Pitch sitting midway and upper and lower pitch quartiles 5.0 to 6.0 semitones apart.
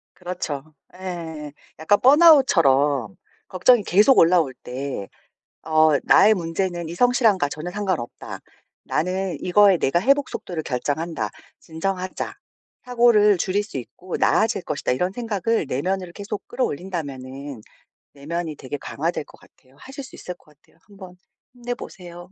Yes: medium, 180 Hz; wide, 5.4 semitones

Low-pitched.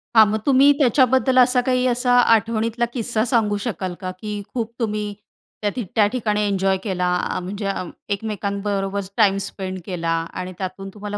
No: high, 210 Hz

